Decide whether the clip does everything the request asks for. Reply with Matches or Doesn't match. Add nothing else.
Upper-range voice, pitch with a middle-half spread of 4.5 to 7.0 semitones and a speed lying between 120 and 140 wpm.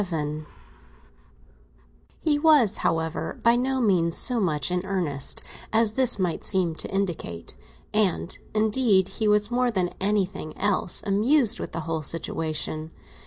Matches